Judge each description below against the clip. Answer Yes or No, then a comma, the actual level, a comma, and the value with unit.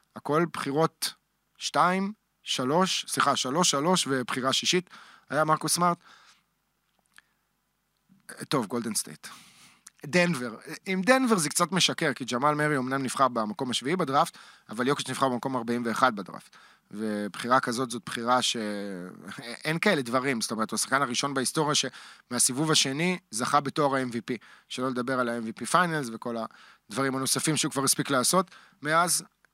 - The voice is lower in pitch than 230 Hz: Yes, low, 135 Hz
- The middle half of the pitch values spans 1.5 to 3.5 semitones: No, average, 4.2 semitones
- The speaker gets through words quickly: No, average, 135 wpm